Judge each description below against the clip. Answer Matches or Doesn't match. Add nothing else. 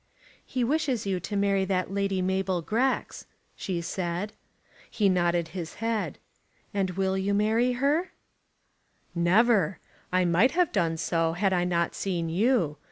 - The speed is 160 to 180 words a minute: Doesn't match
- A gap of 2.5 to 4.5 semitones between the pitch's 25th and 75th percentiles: Matches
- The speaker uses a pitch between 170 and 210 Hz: Matches